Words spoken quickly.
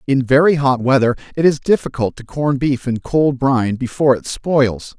No: average, 195 wpm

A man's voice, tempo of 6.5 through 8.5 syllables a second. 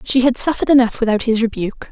No: female; 7.2 syllables/s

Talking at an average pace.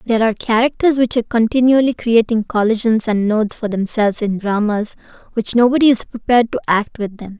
Yes: average, 180 wpm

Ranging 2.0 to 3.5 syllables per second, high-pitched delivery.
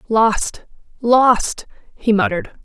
Yes: 3.4 syllables/s; high, 225 Hz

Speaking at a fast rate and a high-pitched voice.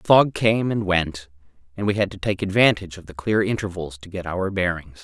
No: fast, 225 wpm; very low, 95 Hz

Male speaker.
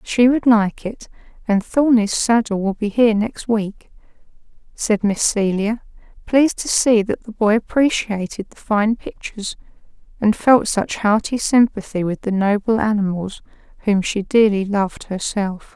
No: female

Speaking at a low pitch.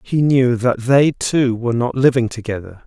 Yes: low, 125 Hz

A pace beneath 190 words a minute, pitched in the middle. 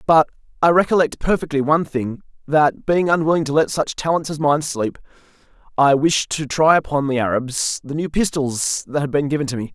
No: average, 195 wpm; medium, 150 Hz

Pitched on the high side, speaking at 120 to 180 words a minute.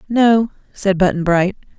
Yes: high, 195 Hz; slow, 135 wpm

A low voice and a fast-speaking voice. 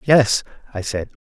No: low, 115 Hz; average, 145 wpm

